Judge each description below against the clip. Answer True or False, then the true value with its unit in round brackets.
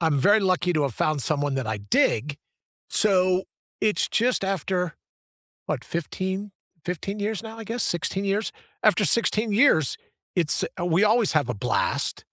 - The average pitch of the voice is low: False (185 Hz)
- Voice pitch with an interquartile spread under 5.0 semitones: False (5.3 semitones)